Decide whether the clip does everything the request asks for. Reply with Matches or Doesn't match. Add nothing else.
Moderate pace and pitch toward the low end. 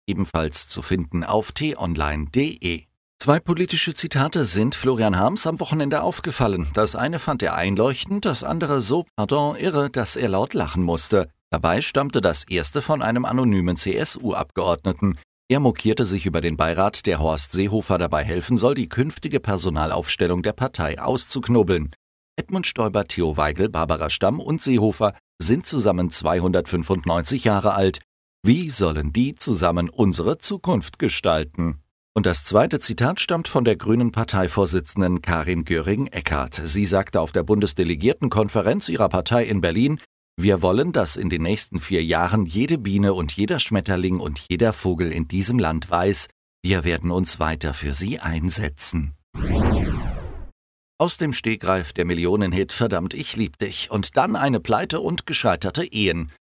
Matches